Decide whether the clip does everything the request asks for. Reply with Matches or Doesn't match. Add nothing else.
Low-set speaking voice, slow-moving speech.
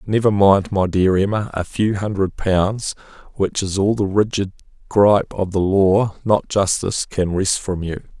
Doesn't match